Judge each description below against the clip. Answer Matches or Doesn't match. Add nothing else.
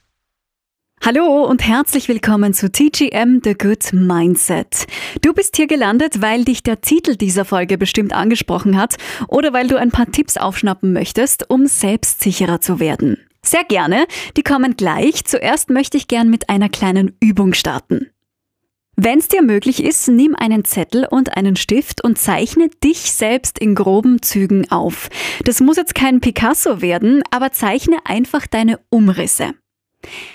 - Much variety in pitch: Matches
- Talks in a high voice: Matches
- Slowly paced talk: Doesn't match